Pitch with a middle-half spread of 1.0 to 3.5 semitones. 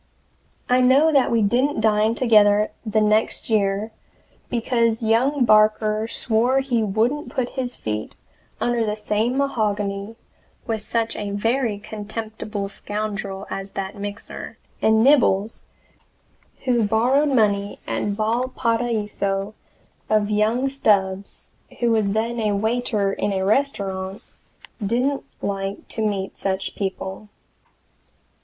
Yes: average, 2.8 semitones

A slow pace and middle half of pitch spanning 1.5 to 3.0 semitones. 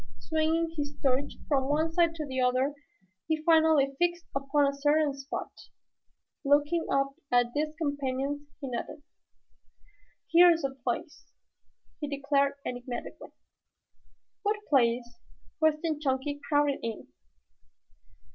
Yes: slow, 120 wpm; narrow, 2.6 semitones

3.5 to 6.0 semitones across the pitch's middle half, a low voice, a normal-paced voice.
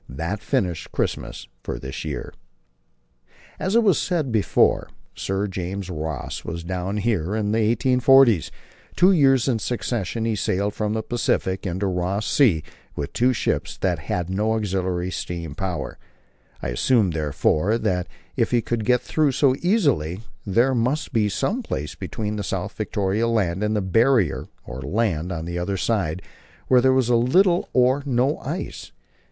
Yes: wide, 5.6 semitones; low, 105 Hz; average, 160 wpm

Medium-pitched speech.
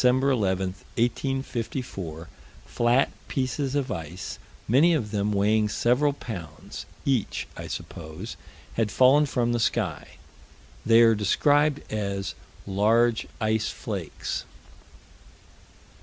No: low, 115 Hz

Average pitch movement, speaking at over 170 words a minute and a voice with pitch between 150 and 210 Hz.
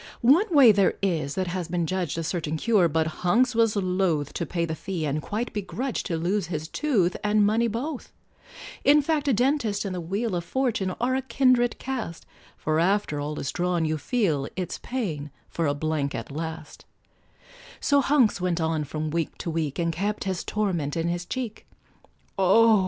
No: wide, 6.1 semitones; average, 190 wpm; medium, 185 Hz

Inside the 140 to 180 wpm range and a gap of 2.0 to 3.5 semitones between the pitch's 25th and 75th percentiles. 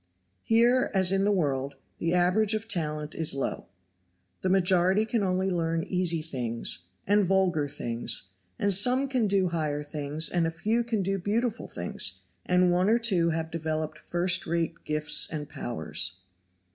No: average, 160 wpm; average, 4.4 semitones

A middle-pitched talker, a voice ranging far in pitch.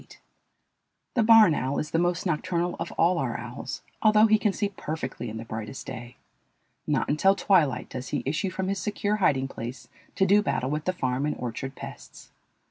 Yes: medium, 165 Hz; wide, 6.8 semitones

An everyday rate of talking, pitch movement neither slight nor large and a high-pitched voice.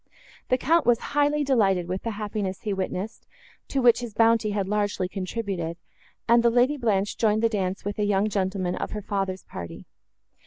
Yes: average, 185 wpm; average, 3.3 semitones; high, 210 Hz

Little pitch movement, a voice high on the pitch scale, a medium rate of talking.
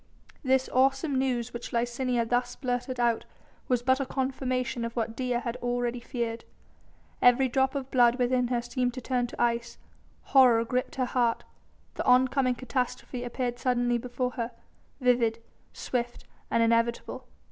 Yes: narrow, 1.4 semitones; high, 245 Hz; average, 150 wpm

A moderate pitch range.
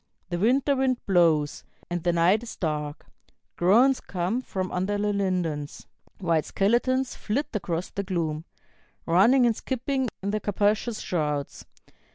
No: wide, 5.7 semitones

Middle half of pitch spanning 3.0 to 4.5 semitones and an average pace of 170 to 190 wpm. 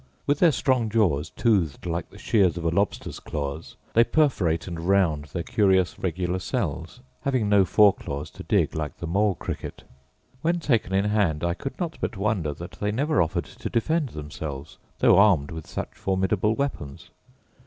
No: average, 5.2 semitones; average, 175 wpm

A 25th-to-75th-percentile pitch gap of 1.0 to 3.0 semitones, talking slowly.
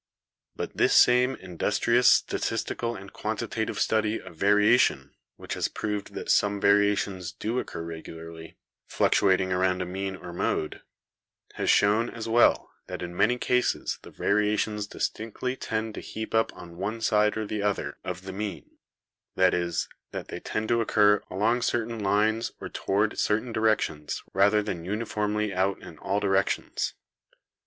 No: average, 2.7 semitones; average, 160 wpm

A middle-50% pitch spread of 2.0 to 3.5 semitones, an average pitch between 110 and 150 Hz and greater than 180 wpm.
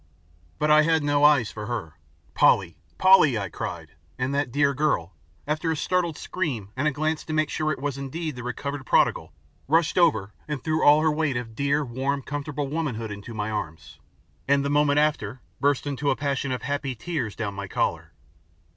No: average, 3.9 semitones; medium, 140 Hz; average, 190 wpm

